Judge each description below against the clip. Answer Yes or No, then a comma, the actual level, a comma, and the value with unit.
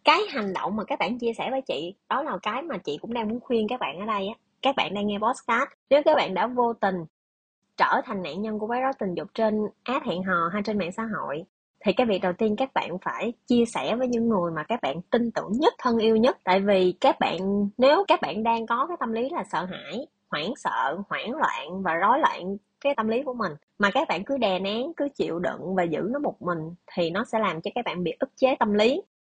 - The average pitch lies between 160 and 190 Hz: No, high, 225 Hz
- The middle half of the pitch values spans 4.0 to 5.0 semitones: Yes, average, 4.6 semitones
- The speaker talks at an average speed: No, fast, 260 wpm